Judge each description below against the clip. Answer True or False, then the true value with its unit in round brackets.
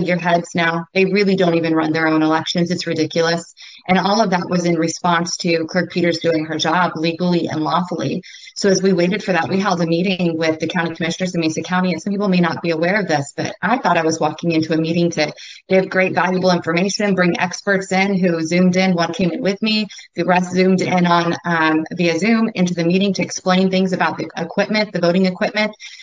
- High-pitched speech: False (175 Hz)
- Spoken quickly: True (230 wpm)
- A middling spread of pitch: False (2.1 semitones)